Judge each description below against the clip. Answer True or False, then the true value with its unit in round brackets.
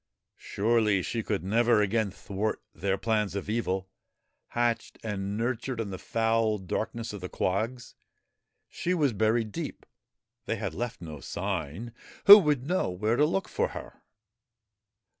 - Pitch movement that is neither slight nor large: True (3.3 semitones)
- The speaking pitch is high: False (110 Hz)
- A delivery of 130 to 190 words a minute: True (145 wpm)